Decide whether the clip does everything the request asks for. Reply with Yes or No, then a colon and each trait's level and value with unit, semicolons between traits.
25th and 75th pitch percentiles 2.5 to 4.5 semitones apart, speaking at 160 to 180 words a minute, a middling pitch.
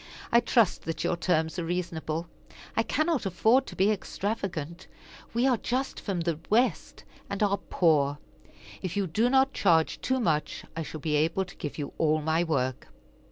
No: wide, 5.5 semitones; average, 175 wpm; medium, 175 Hz